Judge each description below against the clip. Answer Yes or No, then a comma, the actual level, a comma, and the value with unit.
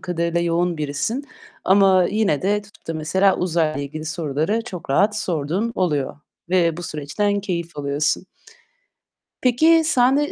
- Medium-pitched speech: Yes, medium, 175 Hz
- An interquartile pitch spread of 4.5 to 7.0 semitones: Yes, average, 4.8 semitones